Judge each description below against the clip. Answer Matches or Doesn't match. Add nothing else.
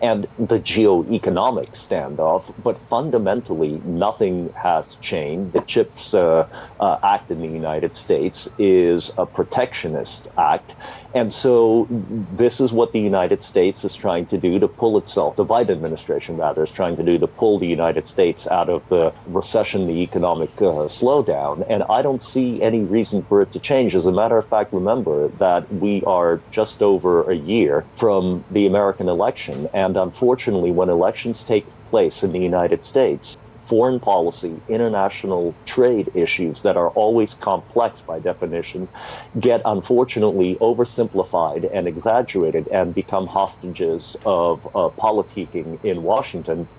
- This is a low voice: Matches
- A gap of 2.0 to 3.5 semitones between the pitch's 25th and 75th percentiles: Doesn't match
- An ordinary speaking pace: Matches